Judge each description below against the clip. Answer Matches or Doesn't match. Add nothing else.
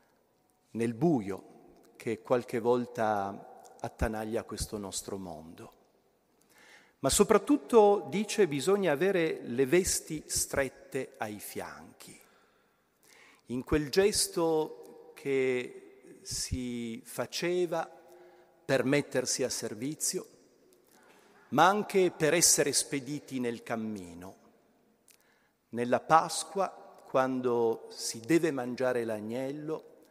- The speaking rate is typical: Doesn't match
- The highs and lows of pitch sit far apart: Matches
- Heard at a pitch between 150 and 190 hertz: Doesn't match